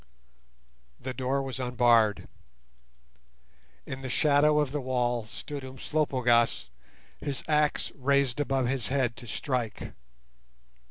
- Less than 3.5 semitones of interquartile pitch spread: Yes, narrow, 2.5 semitones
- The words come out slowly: Yes, slow, 110 wpm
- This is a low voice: Yes, low, 130 Hz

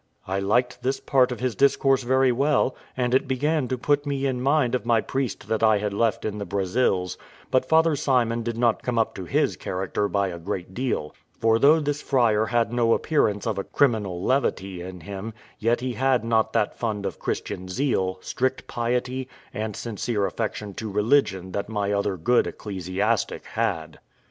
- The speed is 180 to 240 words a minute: Yes, average, 190 wpm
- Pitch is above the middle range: No, low, 115 Hz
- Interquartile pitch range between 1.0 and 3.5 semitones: No, average, 4.3 semitones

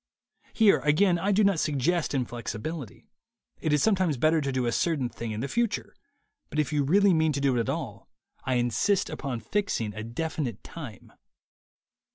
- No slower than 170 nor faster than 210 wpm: Yes, average, 180 wpm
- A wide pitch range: Yes, wide, 6.0 semitones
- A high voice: No, medium, 150 Hz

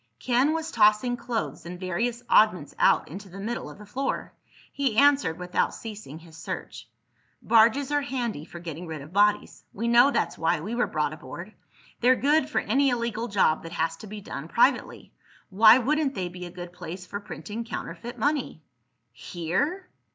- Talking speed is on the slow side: No, average, 180 wpm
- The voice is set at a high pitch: Yes, high, 210 Hz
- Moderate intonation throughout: No, wide, 6.1 semitones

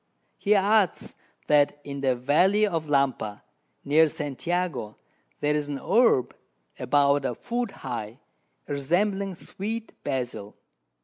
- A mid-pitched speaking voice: Yes, medium, 150 Hz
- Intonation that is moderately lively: No, wide, 6.2 semitones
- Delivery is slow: Yes, slow, 115 wpm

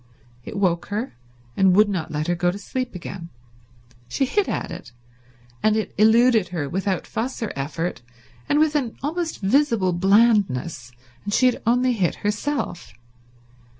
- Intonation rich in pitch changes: Yes, wide, 5.9 semitones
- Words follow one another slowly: No, average, 155 wpm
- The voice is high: Yes, high, 205 Hz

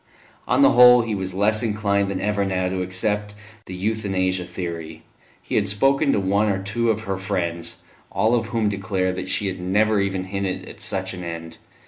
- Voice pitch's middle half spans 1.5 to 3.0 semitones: Yes, narrow, 2.4 semitones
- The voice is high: No, low, 100 Hz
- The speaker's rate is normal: Yes, average, 195 wpm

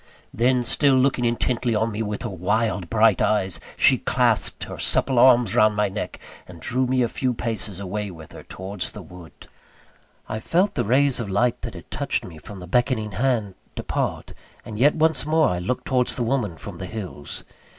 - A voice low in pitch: Yes, low, 110 Hz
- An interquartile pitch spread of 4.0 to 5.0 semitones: Yes, average, 4.4 semitones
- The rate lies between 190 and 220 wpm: Yes, average, 195 wpm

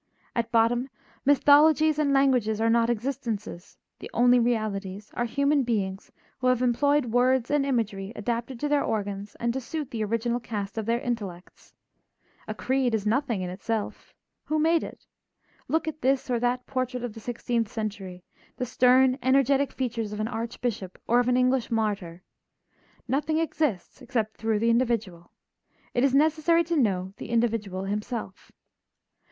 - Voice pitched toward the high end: Yes, high, 235 Hz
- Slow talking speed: No, average, 160 wpm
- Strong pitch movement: No, average, 3.5 semitones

